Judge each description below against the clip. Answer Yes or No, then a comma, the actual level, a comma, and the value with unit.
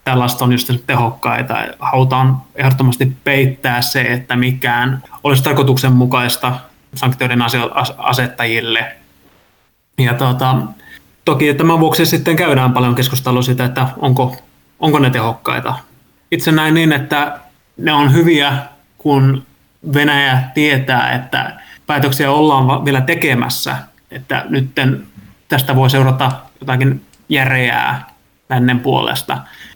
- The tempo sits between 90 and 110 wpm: Yes, average, 105 wpm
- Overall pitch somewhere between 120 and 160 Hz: Yes, low, 130 Hz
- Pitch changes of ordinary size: No, narrow, 2.2 semitones